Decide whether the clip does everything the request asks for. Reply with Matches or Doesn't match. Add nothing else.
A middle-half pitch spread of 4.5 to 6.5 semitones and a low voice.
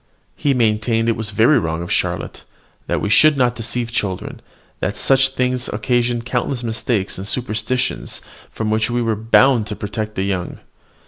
Doesn't match